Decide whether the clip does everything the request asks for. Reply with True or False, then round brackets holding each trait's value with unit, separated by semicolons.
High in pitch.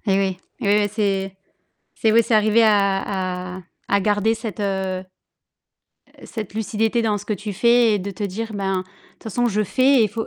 True (205 Hz)